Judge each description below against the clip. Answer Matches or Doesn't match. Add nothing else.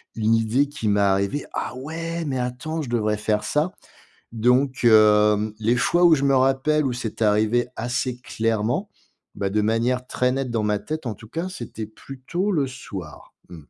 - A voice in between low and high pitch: Doesn't match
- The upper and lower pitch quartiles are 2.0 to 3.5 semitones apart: Doesn't match